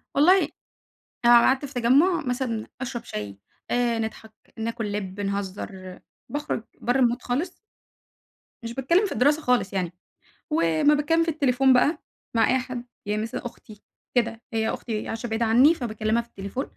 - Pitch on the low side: No, high, 235 Hz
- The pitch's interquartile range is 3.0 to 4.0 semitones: Yes, average, 3.6 semitones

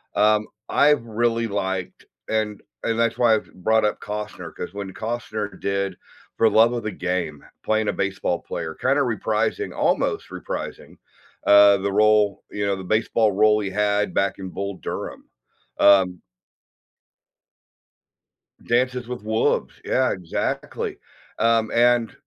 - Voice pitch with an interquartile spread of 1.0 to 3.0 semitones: Yes, narrow, 2.6 semitones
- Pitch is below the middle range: Yes, low, 105 Hz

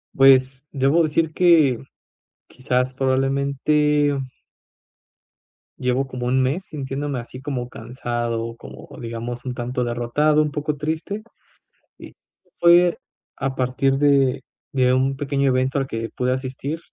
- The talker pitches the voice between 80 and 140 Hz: Yes, low, 135 Hz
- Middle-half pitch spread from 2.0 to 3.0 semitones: Yes, narrow, 2.5 semitones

